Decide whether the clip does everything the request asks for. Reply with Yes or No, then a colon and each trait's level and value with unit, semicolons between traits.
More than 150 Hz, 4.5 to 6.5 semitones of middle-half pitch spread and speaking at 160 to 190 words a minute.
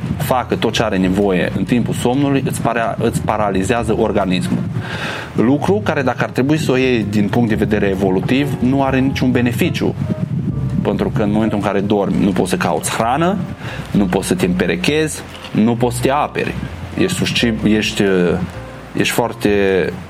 No: low, 120 Hz; average, 4.8 semitones; average, 165 wpm